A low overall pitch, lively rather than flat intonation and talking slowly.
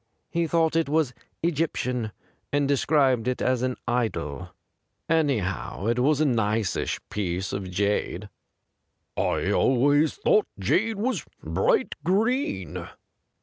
Yes: low, 130 Hz; wide, 6.8 semitones; slow, 120 wpm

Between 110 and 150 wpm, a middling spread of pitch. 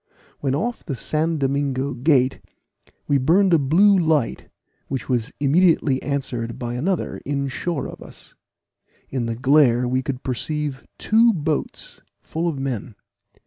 Yes: average, 145 wpm; average, 3.6 semitones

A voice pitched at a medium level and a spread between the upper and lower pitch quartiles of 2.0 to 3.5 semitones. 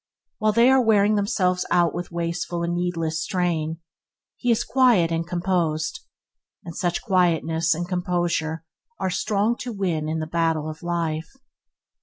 Yes: medium, 175 Hz; average, 3.2 semitones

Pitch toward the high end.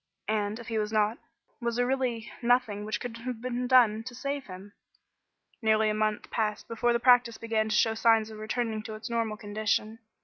Yes: high, 225 Hz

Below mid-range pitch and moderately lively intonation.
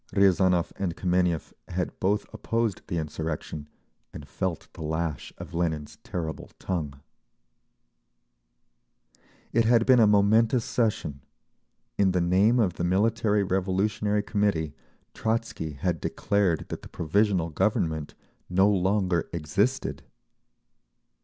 Yes: very low, 95 Hz; average, 4.0 semitones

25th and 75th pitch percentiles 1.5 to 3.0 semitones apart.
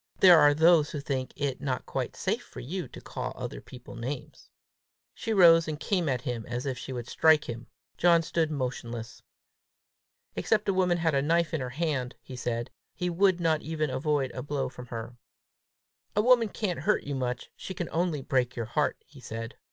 No: average, 5.1 semitones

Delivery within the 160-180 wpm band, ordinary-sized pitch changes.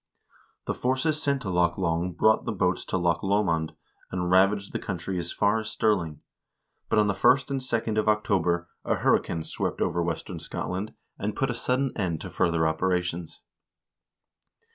Yes: average, 170 wpm; average, 4.0 semitones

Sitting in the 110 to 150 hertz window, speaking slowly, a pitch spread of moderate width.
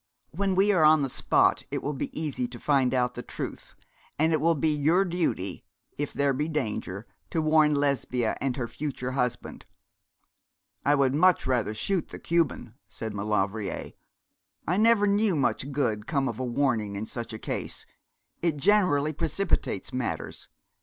No: medium, 140 Hz; average, 165 wpm; average, 4.7 semitones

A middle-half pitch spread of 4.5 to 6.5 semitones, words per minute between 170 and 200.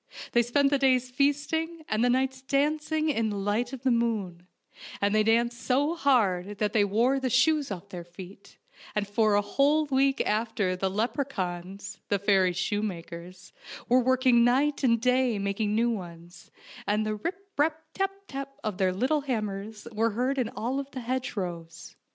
Yes: average, 5.0 semitones; average, 175 wpm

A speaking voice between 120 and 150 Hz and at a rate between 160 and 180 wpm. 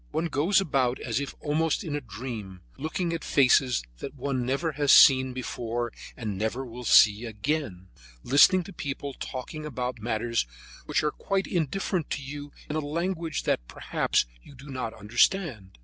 Yes: low, 135 Hz; average, 165 wpm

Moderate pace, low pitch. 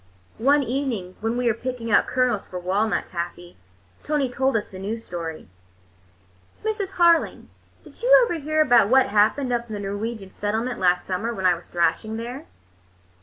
No: average, 170 wpm; high, 230 Hz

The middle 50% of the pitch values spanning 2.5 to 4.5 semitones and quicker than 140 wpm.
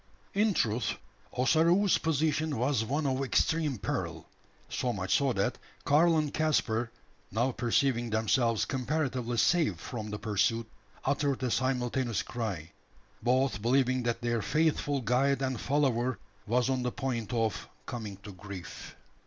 No: average, 3.6 semitones; slow, 135 wpm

